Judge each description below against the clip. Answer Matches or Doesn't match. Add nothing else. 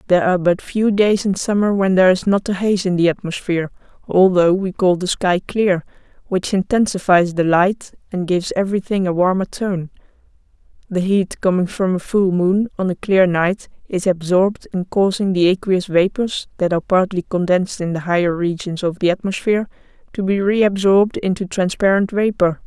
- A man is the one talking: Doesn't match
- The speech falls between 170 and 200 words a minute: Matches